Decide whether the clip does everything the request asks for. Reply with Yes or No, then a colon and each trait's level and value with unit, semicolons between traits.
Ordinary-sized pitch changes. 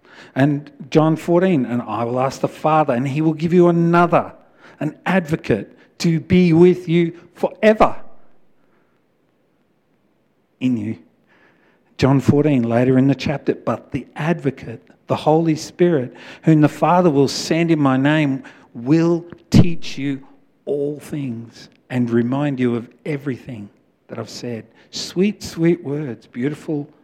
Yes: average, 4.3 semitones